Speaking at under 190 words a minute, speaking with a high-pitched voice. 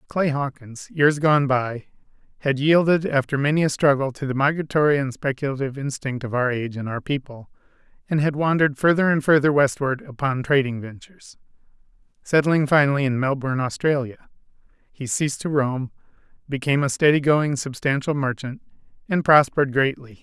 No: average, 150 wpm; medium, 140 Hz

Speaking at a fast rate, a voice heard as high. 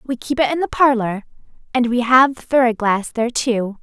Yes: fast, 220 wpm; high, 240 Hz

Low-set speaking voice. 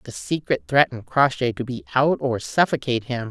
Yes: low, 130 Hz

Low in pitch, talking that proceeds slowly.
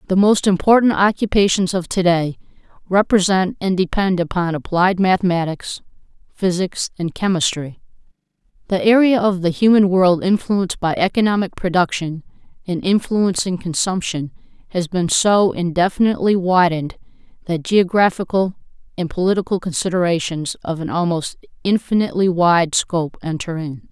No: medium, 180 Hz; slow, 115 wpm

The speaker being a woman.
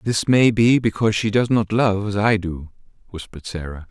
No: male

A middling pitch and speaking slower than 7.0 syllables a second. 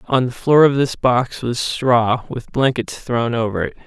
No: low, 125 Hz; 4.1 syllables/s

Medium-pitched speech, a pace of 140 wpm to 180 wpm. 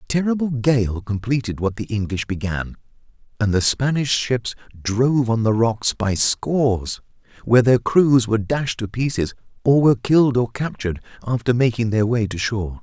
No: low, 115 Hz; average, 170 wpm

